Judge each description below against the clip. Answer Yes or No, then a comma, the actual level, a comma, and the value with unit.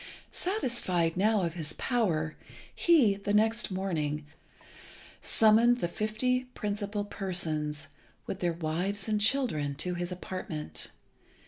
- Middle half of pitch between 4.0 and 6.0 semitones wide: Yes, average, 5.0 semitones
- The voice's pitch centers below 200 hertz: Yes, high, 190 Hz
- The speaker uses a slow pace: Yes, slow, 115 wpm